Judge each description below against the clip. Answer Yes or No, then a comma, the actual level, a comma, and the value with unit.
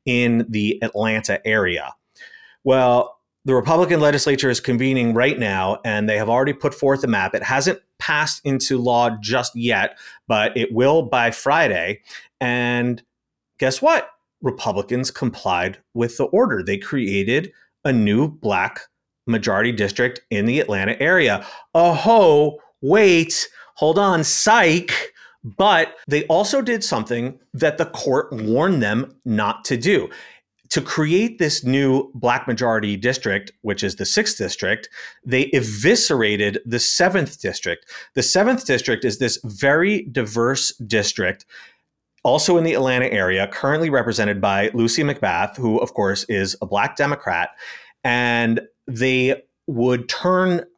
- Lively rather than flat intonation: No, average, 4.3 semitones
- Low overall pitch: Yes, low, 125 Hz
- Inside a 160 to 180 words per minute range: No, slow, 135 wpm